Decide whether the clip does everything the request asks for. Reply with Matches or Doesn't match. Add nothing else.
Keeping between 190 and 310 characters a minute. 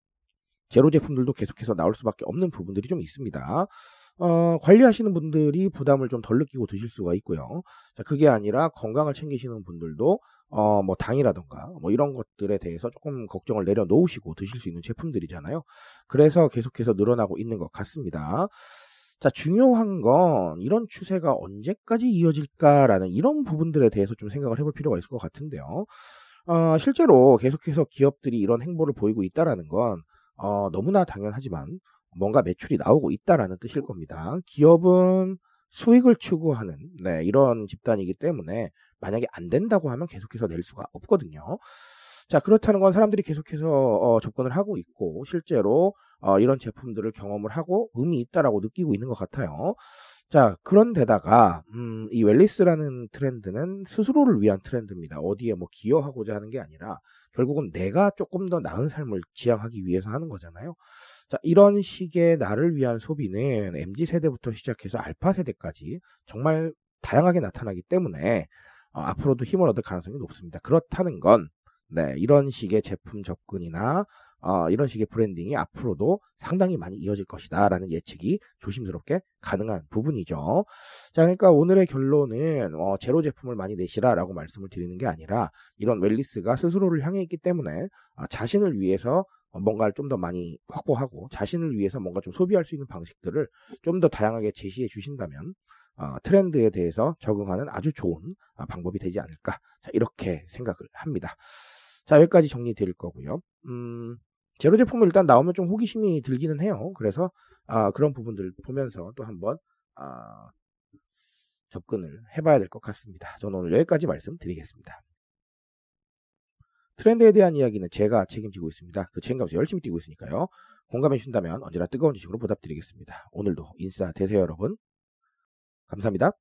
Doesn't match